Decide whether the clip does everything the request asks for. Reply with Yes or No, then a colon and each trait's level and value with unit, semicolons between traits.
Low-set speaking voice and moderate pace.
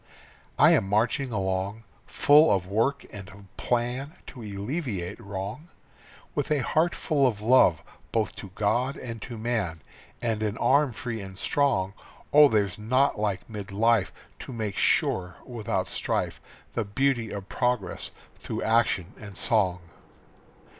Yes: low, 110 Hz; average, 145 wpm